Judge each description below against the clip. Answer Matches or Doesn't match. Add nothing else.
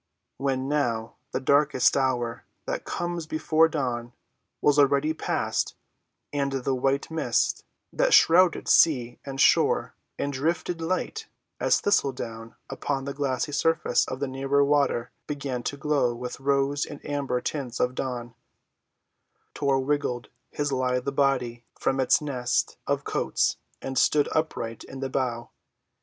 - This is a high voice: Doesn't match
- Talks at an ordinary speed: Matches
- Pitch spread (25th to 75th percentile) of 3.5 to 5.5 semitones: Doesn't match